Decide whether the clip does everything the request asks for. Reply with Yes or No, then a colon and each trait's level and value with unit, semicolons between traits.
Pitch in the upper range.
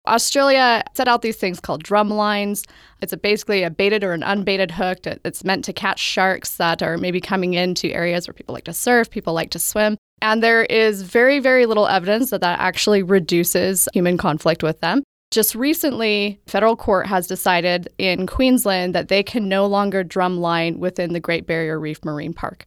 Yes: high, 195 Hz